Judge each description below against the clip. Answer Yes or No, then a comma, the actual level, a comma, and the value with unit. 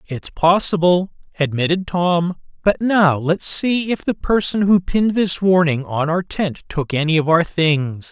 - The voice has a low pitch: No, medium, 170 Hz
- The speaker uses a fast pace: No, average, 170 wpm